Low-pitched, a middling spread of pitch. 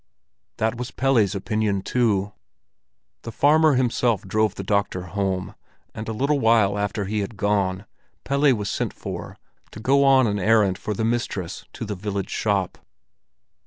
Yes: low, 105 Hz; average, 3.3 semitones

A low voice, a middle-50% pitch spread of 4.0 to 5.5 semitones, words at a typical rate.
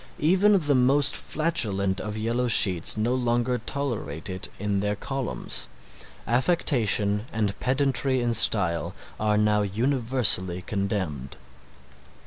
No: low, 110 Hz; average, 4.7 semitones; slow, 115 wpm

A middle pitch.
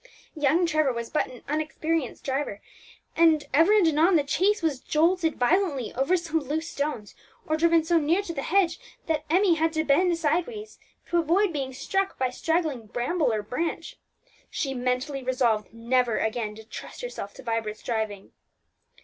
No: very high, 305 Hz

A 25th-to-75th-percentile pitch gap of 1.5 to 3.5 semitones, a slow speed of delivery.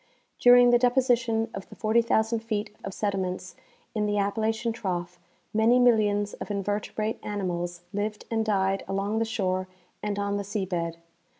No: narrow, 2.4 semitones; average, 155 wpm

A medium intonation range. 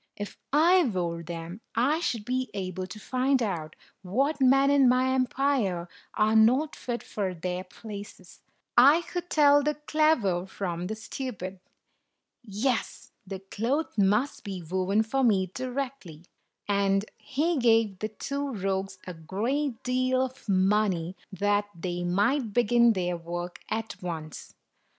No: wide, 5.8 semitones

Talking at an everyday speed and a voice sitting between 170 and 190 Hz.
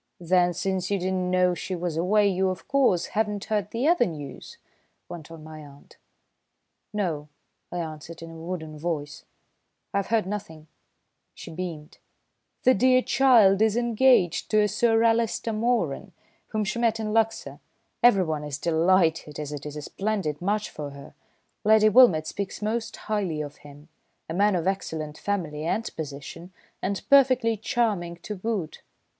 Yes: average, 160 wpm; medium, 185 Hz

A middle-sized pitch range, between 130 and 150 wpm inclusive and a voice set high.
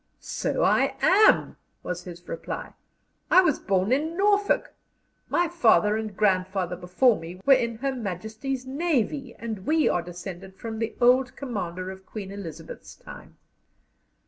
No: wide, 6.4 semitones; average, 145 wpm; high, 220 Hz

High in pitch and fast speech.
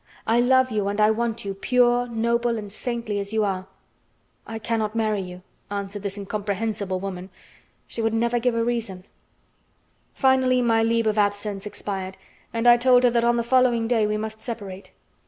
No: high, 225 Hz; average, 180 wpm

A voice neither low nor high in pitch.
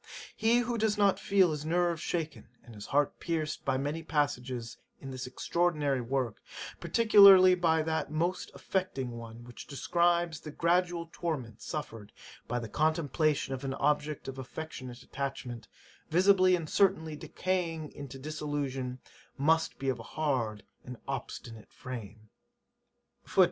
Yes: medium, 150 Hz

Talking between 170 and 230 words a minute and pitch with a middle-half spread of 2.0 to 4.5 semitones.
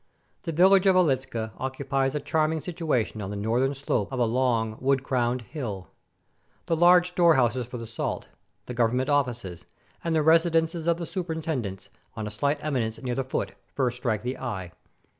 No: average, 180 wpm; wide, 5.4 semitones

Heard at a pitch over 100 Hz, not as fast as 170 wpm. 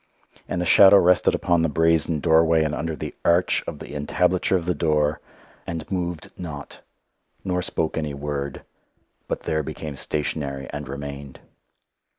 No: very low, 80 Hz; average, 155 wpm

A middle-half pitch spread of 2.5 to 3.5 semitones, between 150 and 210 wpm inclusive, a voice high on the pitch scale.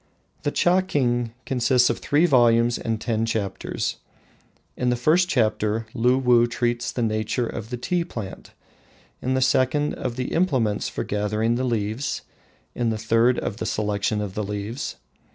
No: average, 2.9 semitones; average, 160 wpm; low, 120 Hz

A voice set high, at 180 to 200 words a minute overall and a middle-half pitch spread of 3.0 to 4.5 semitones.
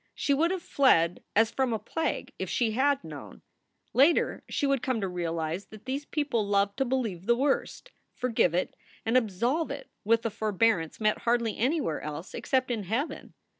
No: high, 230 Hz; average, 185 wpm; average, 5.1 semitones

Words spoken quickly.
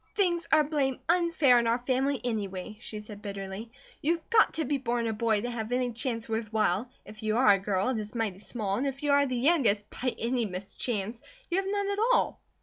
Yes: fast, 230 wpm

